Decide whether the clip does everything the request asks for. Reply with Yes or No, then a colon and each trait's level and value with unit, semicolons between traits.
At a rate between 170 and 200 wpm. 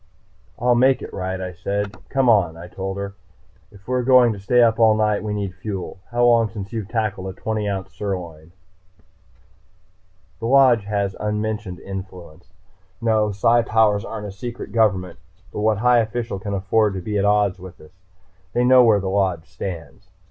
Yes: average, 180 wpm